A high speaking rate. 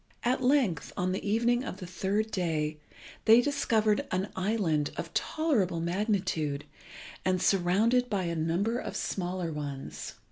No: average, 140 wpm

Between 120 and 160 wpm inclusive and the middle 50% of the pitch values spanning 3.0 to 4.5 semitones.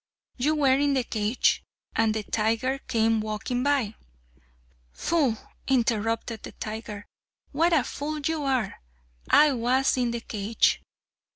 Yes: slow, 135 wpm; average, 3.9 semitones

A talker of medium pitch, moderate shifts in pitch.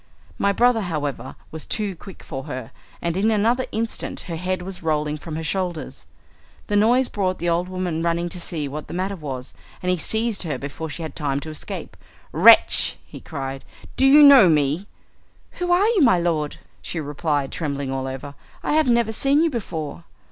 No: medium, 175 Hz; wide, 6.0 semitones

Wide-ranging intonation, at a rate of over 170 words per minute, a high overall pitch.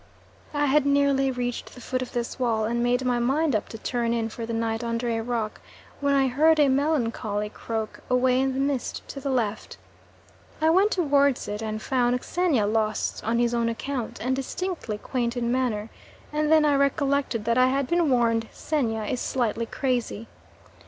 No: average, 3.4 semitones; average, 190 wpm; very high, 250 Hz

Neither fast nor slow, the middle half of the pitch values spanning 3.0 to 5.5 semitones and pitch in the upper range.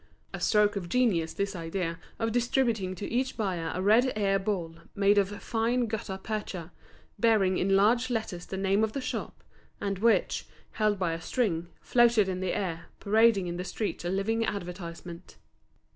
Yes: average, 175 wpm; average, 3.5 semitones; high, 200 Hz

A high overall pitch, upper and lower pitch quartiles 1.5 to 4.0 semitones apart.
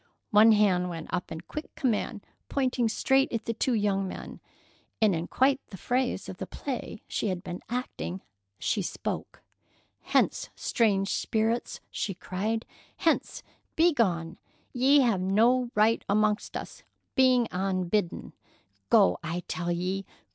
No: high, 210 Hz; average, 5.0 semitones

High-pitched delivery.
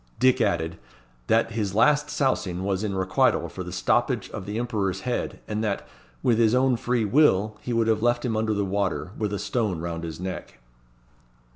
No: low, 105 Hz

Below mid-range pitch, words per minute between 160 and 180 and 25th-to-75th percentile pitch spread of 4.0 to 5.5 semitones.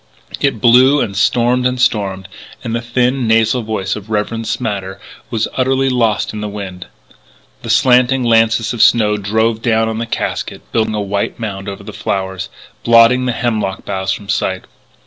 No: low, 110 Hz; average, 170 wpm; average, 3.0 semitones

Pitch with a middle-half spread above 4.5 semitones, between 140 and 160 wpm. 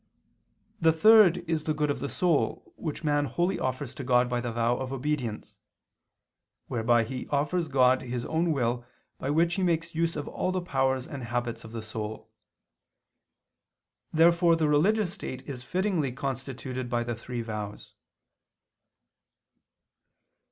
Yes: average, 5.2 semitones; average, 150 wpm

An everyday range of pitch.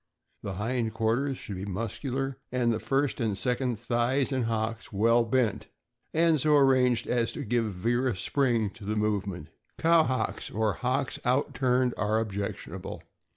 Yes: average, 3.2 semitones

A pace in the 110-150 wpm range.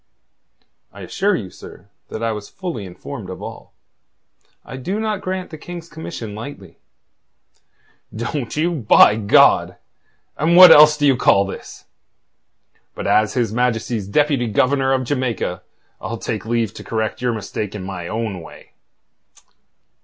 Yes: average, 145 wpm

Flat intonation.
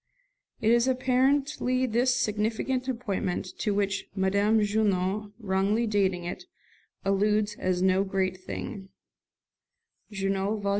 No: average, 3.4 semitones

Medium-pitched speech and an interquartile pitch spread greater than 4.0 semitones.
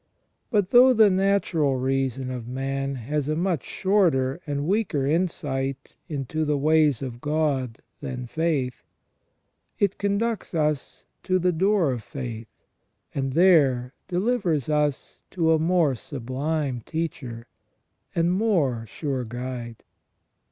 Yes: medium, 150 Hz; average, 5.2 semitones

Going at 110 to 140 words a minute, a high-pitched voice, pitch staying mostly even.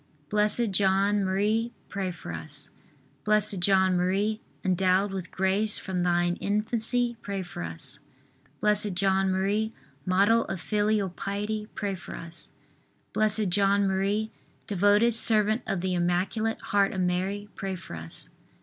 Yes: slow, 135 wpm; high, 195 Hz; narrow, 2.3 semitones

